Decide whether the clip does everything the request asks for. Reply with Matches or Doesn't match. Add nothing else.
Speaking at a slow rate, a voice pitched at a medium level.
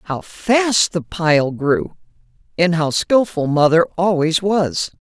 Matches